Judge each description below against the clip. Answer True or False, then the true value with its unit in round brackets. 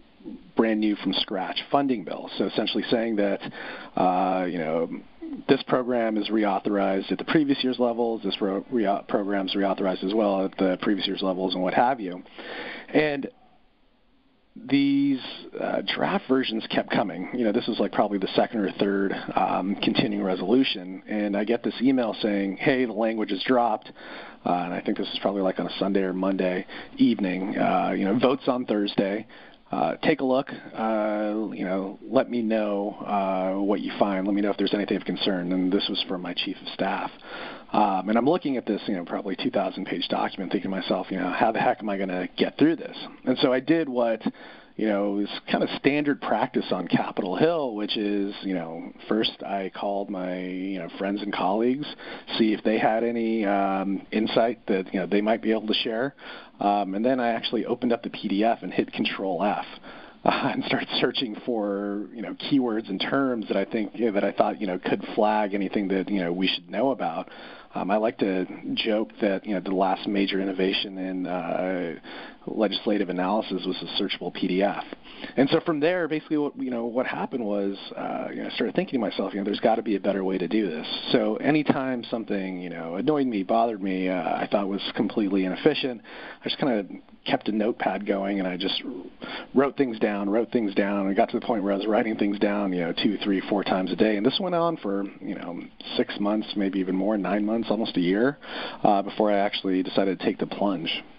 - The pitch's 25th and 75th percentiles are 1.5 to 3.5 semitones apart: False (3.9 semitones)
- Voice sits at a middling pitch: False (105 Hz)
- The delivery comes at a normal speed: False (215 wpm)